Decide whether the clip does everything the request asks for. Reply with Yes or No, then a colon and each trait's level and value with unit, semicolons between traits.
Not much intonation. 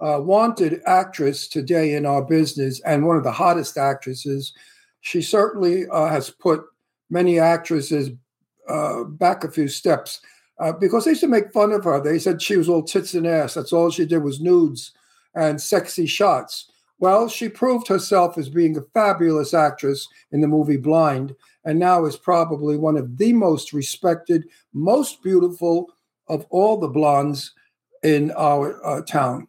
No: average, 3.8 semitones